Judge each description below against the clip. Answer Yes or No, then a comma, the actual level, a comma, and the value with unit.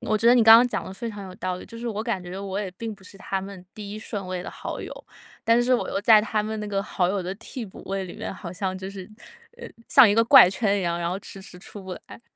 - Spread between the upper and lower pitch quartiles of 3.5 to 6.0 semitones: No, average, 2.8 semitones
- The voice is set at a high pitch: Yes, high, 200 Hz